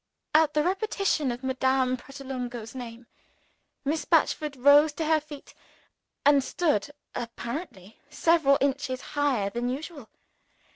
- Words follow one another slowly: Yes, slow, 115 wpm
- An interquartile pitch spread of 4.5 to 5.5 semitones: No, average, 3.5 semitones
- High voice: Yes, very high, 275 Hz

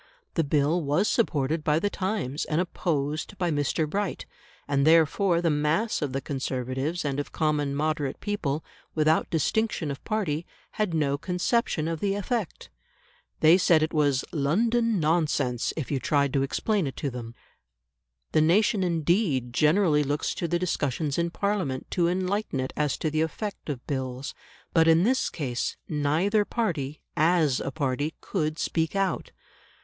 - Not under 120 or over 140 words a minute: No, average, 160 wpm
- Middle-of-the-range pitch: Yes, medium, 155 Hz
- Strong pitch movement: No, average, 4.1 semitones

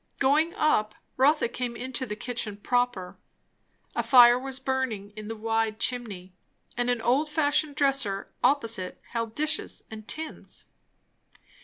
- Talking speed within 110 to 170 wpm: Yes, slow, 135 wpm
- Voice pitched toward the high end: Yes, high, 245 Hz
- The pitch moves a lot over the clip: No, average, 3.8 semitones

